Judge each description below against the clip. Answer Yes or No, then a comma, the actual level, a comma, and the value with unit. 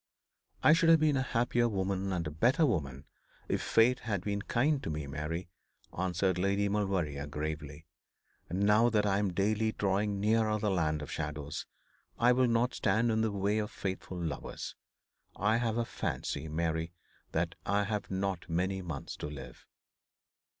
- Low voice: Yes, low, 100 Hz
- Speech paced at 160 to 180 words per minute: Yes, average, 170 wpm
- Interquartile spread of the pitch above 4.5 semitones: Yes, average, 5.1 semitones